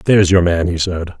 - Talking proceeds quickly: Yes, fast, 250 wpm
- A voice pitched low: Yes, very low, 90 Hz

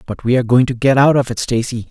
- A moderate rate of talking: No, fast, 285 wpm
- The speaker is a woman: No, male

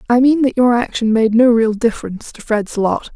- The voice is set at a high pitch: Yes, high, 230 Hz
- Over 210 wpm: Yes, fast, 230 wpm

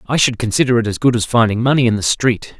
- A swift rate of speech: Yes, fast, 275 wpm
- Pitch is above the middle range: No, low, 115 Hz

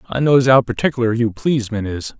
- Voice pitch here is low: Yes, low, 120 Hz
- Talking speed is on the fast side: No, average, 190 wpm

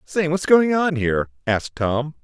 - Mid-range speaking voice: Yes, medium, 145 Hz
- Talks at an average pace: Yes, average, 160 wpm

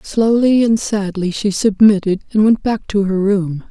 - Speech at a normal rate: Yes, average, 180 wpm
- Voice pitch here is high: Yes, high, 205 Hz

